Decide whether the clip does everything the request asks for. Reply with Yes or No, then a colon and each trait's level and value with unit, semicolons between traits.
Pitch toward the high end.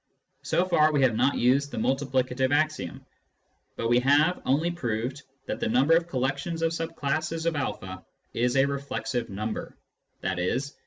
No: medium, 140 Hz